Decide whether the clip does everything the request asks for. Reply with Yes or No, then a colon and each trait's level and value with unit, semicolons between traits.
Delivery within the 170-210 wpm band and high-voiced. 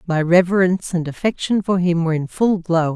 No: fast, 205 wpm; medium, 175 Hz